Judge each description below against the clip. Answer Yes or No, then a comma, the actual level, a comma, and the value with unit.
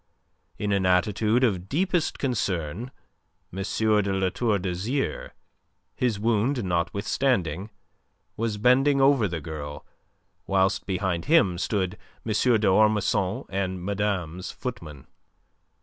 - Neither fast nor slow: No, slow, 105 wpm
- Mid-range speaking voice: No, low, 100 Hz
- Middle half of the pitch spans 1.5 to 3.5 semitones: No, average, 4.3 semitones